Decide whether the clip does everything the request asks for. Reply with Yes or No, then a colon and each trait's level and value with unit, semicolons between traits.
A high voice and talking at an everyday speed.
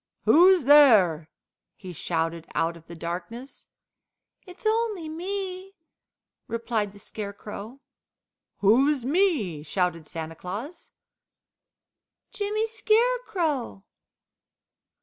No: high, 245 Hz; slow, 85 wpm